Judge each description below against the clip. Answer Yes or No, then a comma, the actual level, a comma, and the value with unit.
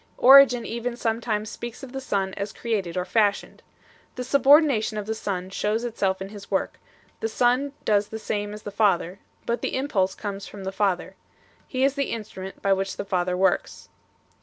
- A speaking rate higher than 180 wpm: Yes, average, 190 wpm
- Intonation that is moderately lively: Yes, average, 3.7 semitones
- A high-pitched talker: Yes, high, 210 Hz